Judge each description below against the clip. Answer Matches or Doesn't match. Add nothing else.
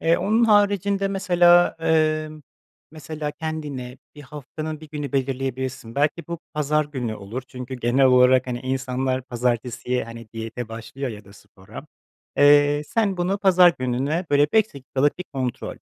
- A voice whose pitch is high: Doesn't match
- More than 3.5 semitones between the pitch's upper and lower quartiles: Matches